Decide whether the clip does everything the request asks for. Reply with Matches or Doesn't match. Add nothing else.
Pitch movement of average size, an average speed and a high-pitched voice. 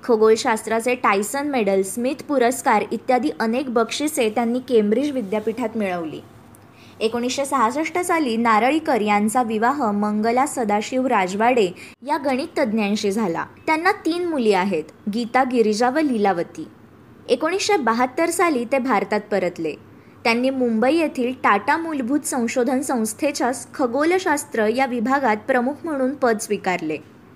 Matches